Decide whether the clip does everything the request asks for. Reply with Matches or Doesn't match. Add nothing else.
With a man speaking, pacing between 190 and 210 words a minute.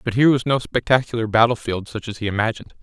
Doesn't match